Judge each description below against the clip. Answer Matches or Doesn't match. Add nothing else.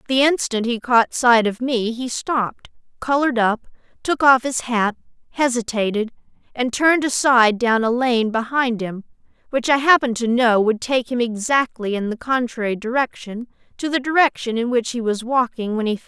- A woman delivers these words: Matches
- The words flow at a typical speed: Matches